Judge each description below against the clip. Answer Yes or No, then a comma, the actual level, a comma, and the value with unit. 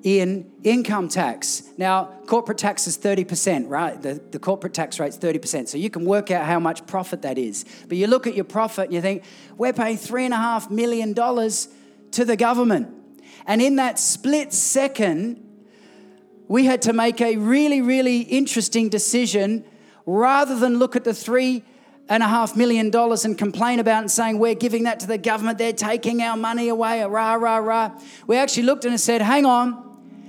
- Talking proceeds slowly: No, average, 200 wpm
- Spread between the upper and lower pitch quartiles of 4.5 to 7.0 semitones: No, average, 3.5 semitones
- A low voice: No, high, 225 Hz